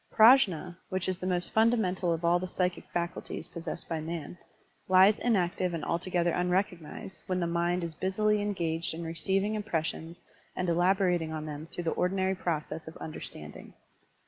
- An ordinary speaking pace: Yes, average, 165 wpm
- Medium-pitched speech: Yes, medium, 175 Hz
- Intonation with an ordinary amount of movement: No, narrow, 2.1 semitones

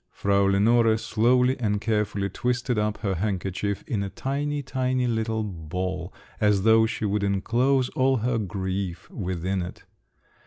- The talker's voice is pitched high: No, low, 105 Hz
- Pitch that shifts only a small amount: No, average, 3.8 semitones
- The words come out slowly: No, average, 145 wpm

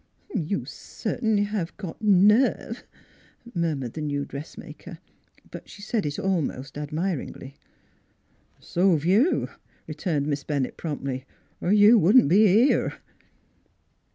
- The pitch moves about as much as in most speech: No, wide, 6.1 semitones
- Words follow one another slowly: Yes, slow, 130 wpm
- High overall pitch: No, medium, 170 Hz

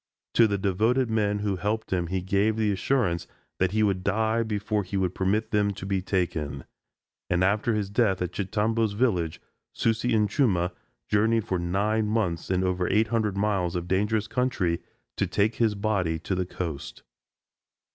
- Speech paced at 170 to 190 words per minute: Yes, average, 175 wpm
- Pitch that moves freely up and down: No, average, 3.1 semitones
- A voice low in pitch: Yes, low, 100 Hz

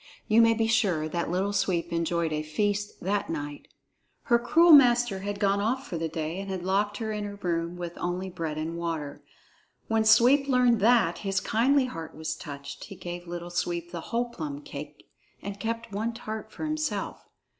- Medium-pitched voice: No, high, 195 Hz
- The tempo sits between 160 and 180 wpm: No, average, 195 wpm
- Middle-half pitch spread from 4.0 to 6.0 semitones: Yes, average, 5.1 semitones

